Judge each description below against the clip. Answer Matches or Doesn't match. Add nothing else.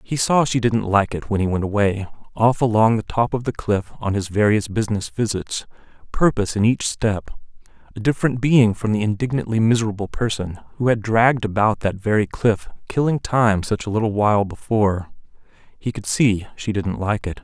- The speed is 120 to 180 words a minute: Doesn't match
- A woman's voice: Doesn't match